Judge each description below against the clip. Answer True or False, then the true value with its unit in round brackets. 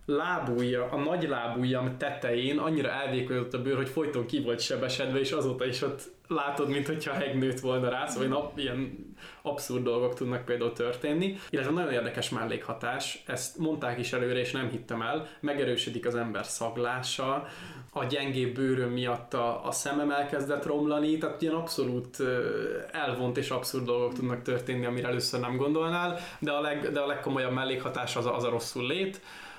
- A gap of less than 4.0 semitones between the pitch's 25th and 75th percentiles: True (2.9 semitones)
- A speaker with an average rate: False (165 wpm)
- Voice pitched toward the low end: True (130 Hz)